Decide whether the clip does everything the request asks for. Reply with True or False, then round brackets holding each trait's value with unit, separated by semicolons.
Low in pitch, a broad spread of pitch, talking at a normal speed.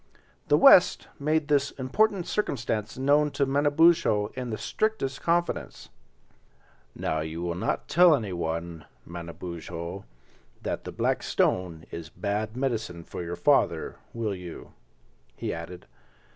False (110 Hz; 8.8 semitones; 125 wpm)